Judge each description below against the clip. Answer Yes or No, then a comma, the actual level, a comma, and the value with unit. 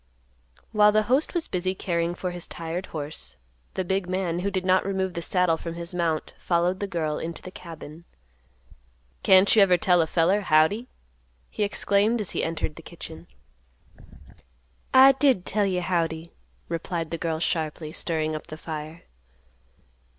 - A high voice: No, medium, 175 Hz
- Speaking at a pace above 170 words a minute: No, average, 165 wpm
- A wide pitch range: No, average, 2.8 semitones